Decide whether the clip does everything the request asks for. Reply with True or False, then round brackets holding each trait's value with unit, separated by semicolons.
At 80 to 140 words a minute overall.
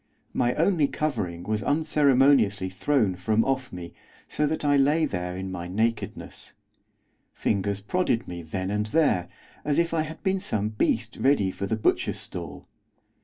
False (160 wpm)